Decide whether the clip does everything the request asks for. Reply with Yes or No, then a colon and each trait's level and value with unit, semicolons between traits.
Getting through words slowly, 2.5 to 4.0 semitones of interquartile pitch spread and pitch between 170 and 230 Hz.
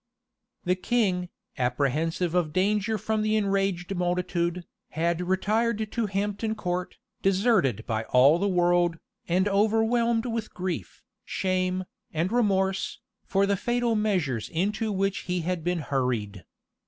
Yes: slow, 130 wpm; average, 3.6 semitones; medium, 185 Hz